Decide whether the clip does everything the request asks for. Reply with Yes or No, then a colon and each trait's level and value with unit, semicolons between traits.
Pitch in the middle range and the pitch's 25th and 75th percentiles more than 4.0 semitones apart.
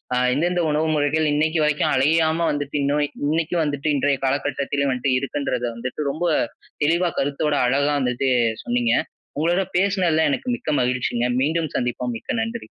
No: medium, 145 Hz; average, 3.0 semitones